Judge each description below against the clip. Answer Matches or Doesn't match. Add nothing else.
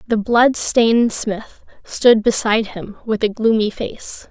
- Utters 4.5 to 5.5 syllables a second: Doesn't match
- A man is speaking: Doesn't match